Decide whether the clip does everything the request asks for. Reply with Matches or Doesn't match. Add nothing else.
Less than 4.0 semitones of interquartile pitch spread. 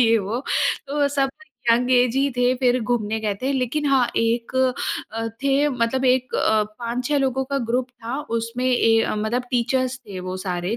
Matches